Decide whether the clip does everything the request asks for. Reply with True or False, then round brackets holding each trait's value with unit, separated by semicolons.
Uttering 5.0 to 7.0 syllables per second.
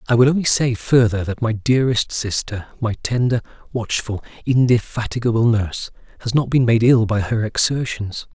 True (5.2 syllables/s)